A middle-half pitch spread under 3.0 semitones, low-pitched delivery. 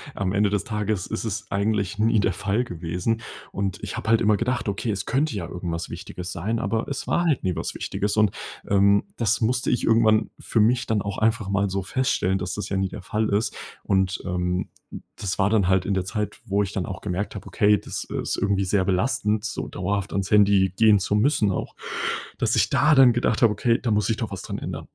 Yes: narrow, 2.6 semitones; low, 100 Hz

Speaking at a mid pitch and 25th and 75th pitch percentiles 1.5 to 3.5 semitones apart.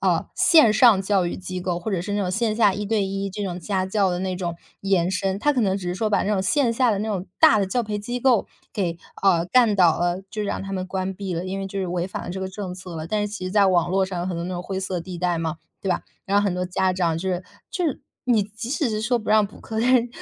No: high, 195 Hz; average, 2.7 semitones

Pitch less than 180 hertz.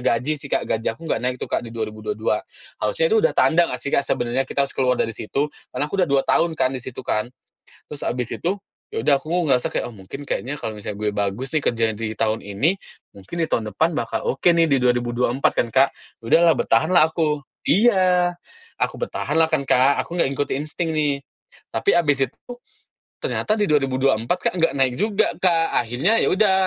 Yes: medium, 140 Hz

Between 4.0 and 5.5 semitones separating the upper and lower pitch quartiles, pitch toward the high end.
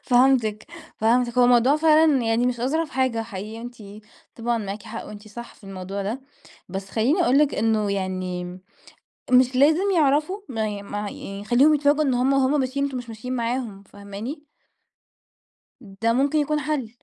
Yes: average, 4.6 semitones; high, 240 Hz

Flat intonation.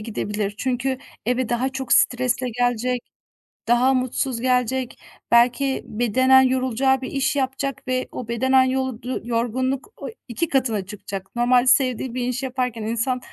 Yes: narrow, 1.7 semitones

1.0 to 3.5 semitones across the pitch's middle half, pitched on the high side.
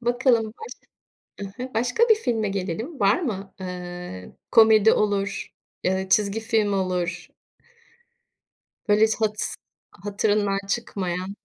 Yes: average, 2.9 semitones; high, 205 Hz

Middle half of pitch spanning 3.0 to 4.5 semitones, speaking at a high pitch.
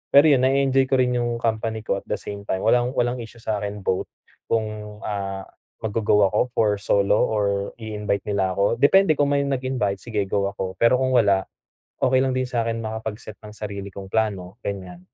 No: average, 3.6 semitones; low, 110 Hz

